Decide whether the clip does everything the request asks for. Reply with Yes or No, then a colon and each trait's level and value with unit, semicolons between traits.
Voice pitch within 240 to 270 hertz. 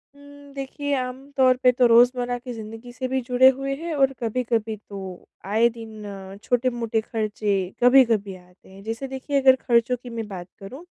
Yes: high, 245 Hz